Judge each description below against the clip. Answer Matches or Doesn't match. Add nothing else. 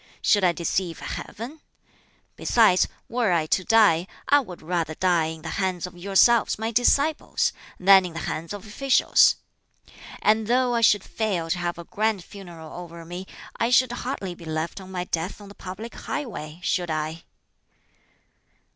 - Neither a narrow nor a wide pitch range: Matches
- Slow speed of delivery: Doesn't match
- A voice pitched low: Doesn't match